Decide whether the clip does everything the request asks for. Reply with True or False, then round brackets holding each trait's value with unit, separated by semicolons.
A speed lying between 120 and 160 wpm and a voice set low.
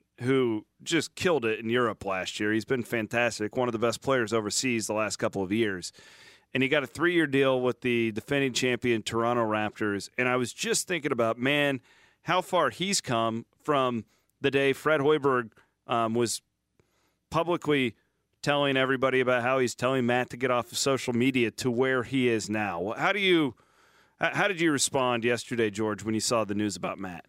False (190 wpm; 125 Hz)